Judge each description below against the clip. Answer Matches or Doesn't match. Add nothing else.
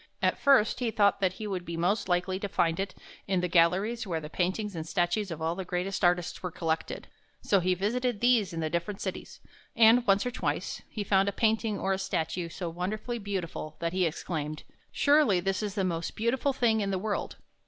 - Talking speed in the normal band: Doesn't match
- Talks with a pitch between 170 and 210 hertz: Matches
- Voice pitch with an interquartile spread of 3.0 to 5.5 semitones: Matches